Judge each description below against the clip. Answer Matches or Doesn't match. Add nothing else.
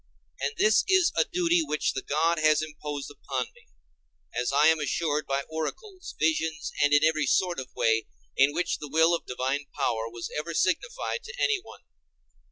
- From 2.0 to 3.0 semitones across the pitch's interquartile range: Doesn't match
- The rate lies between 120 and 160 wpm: Doesn't match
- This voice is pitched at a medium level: Matches